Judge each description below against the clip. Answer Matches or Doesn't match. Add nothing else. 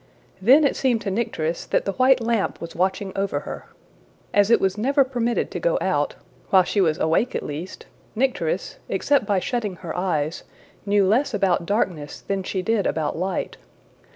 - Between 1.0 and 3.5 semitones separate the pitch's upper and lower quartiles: Doesn't match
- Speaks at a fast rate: Doesn't match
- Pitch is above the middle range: Matches